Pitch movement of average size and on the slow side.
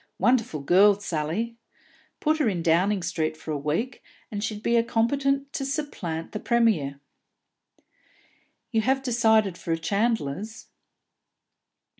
No: wide, 6.2 semitones; slow, 125 wpm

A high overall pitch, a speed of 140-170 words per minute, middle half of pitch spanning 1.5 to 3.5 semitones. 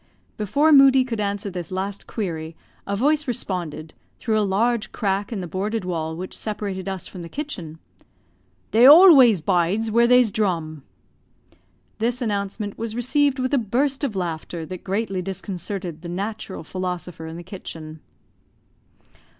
No: high, 200 Hz; average, 150 wpm; average, 4.6 semitones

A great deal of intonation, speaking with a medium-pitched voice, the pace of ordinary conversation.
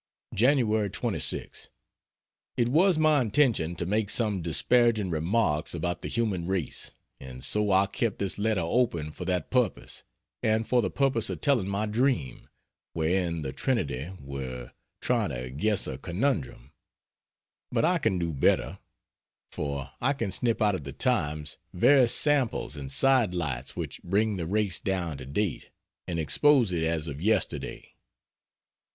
No: wide, 6.7 semitones; very low, 95 Hz; average, 150 wpm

